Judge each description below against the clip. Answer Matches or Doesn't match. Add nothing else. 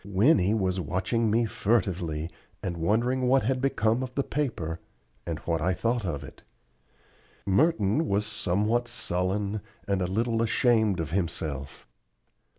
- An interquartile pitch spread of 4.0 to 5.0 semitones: Matches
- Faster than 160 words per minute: Doesn't match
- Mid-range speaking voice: Doesn't match